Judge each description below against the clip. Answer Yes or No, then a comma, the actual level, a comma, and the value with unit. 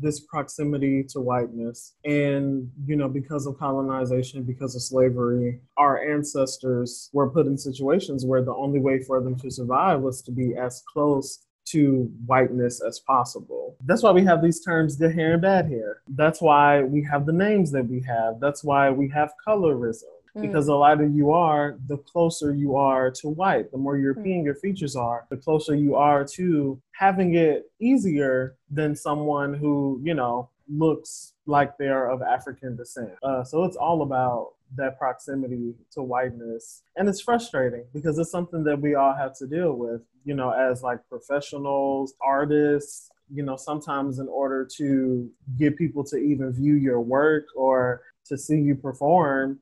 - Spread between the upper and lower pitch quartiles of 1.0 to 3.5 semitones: Yes, narrow, 2.4 semitones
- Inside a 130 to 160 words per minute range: No, average, 175 wpm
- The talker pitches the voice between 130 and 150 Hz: Yes, medium, 140 Hz